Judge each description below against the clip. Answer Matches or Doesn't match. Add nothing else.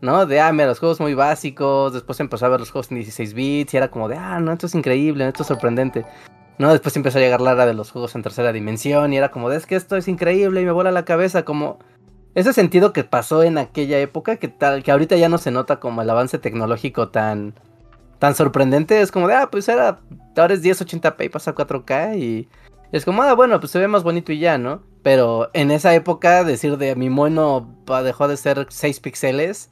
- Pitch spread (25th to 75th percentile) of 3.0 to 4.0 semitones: Doesn't match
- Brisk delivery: Matches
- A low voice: Doesn't match